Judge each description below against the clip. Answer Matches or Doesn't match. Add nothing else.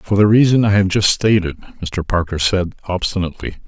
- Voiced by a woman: Doesn't match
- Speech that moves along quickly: Doesn't match